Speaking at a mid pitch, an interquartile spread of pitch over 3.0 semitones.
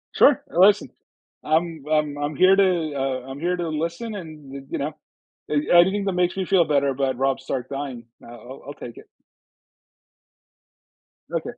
Yes: medium, 155 Hz; average, 4.7 semitones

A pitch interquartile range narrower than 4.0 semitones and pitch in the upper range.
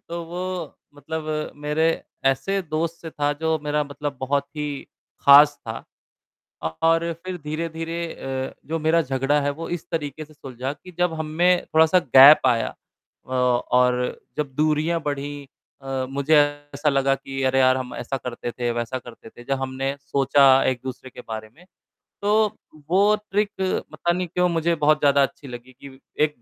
No: average, 3.5 semitones; medium, 145 Hz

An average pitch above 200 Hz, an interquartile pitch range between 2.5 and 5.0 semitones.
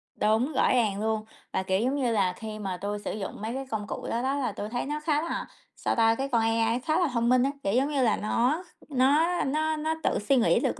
Yes: high, 240 Hz; average, 4.6 semitones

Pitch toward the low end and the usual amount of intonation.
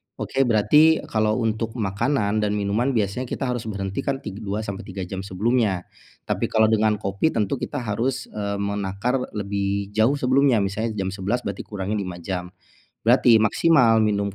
Yes: low, 105 Hz; average, 3.0 semitones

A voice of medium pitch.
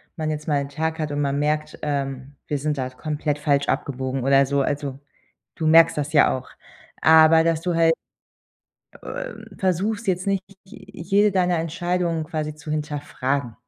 Yes: medium, 155 Hz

